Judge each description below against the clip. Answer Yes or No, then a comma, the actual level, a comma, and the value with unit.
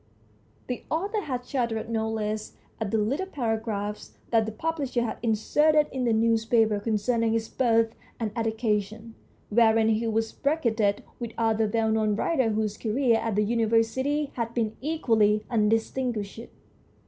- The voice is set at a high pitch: Yes, high, 225 Hz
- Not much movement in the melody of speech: Yes, narrow, 2.1 semitones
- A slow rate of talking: No, average, 145 wpm